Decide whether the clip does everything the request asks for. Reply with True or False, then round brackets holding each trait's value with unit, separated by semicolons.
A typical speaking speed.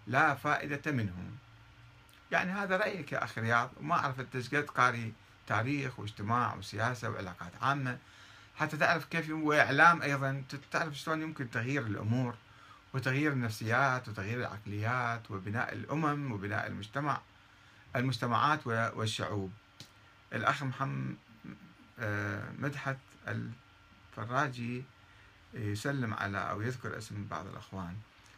True (105 wpm)